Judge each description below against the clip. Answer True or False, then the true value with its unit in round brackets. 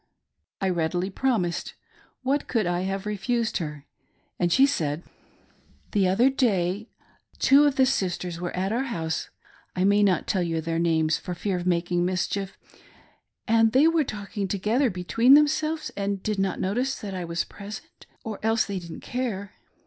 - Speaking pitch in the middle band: False (195 Hz)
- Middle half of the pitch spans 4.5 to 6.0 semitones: True (4.9 semitones)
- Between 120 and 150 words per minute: False (185 wpm)